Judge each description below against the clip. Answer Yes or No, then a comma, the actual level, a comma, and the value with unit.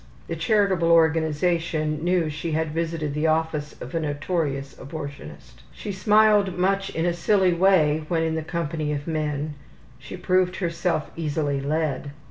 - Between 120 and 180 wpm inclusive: Yes, average, 150 wpm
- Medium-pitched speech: Yes, medium, 160 Hz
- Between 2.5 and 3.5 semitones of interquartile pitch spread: Yes, average, 2.8 semitones